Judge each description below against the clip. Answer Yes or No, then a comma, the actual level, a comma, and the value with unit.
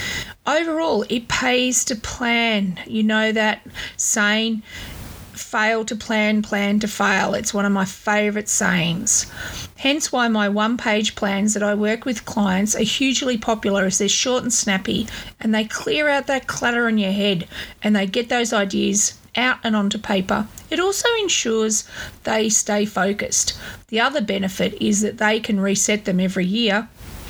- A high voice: Yes, high, 215 Hz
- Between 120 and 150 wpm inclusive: No, average, 165 wpm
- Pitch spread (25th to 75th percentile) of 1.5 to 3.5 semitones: Yes, narrow, 2.6 semitones